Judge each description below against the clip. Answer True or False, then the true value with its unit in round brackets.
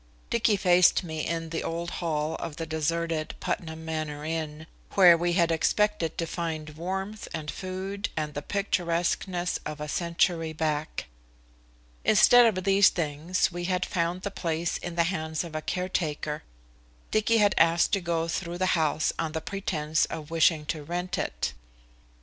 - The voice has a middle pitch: True (170 Hz)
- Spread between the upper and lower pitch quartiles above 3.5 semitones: False (2.6 semitones)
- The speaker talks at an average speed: True (160 wpm)